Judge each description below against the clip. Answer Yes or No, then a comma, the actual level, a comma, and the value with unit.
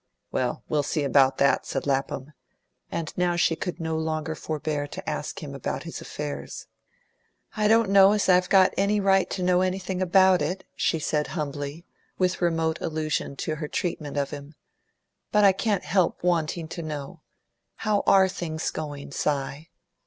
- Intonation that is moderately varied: Yes, average, 4.0 semitones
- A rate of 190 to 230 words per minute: No, average, 165 wpm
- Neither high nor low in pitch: Yes, medium, 160 Hz